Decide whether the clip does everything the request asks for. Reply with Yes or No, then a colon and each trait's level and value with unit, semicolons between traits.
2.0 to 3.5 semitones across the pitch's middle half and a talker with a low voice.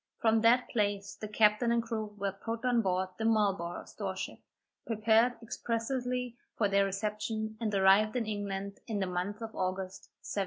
No: narrow, 2.5 semitones; high, 215 Hz